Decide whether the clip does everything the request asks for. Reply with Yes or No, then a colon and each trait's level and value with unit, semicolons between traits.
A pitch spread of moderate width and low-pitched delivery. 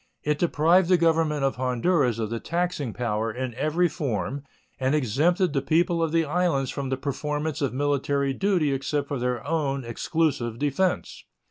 No: average, 4.1 semitones; medium, 145 Hz